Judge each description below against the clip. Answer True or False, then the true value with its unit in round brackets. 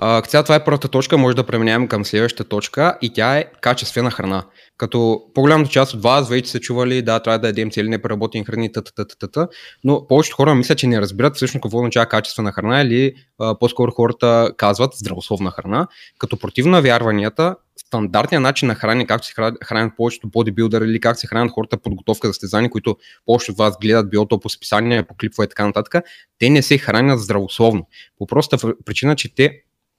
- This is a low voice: True (115 Hz)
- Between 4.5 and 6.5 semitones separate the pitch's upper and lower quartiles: False (2.8 semitones)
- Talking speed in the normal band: False (190 wpm)